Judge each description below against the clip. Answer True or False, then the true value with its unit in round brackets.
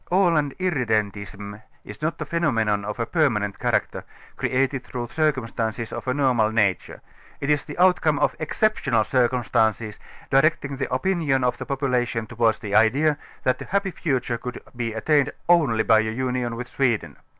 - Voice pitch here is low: True (125 Hz)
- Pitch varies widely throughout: False (4.8 semitones)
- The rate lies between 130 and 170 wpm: True (160 wpm)